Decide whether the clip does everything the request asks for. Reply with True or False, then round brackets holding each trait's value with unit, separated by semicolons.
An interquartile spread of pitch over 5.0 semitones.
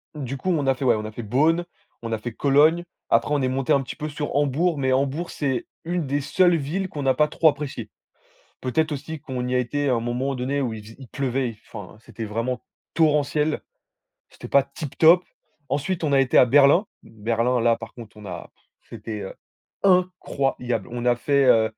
False (3.7 semitones)